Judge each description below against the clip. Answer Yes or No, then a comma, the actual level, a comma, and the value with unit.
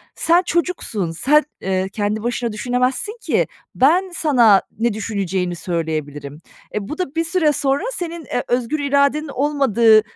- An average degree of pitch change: No, wide, 7.0 semitones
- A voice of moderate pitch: No, high, 245 Hz